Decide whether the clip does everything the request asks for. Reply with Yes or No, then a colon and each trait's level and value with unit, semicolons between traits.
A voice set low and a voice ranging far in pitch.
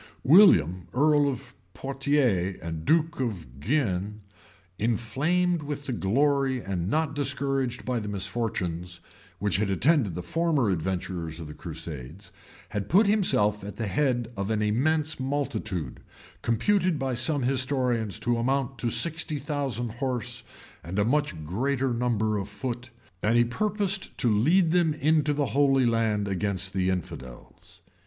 Yes: low, 120 Hz; wide, 6.5 semitones